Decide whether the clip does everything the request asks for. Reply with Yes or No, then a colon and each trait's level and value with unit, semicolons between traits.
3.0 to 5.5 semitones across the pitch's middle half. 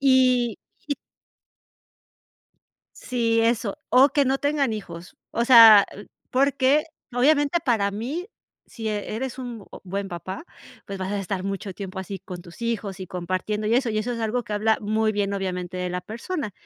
Yes: average, 4.4 semitones